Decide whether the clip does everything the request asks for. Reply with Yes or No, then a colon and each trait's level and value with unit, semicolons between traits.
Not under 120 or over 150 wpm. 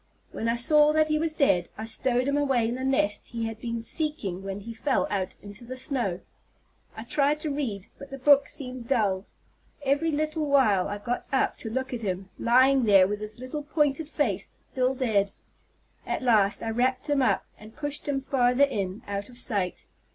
No: average, 200 wpm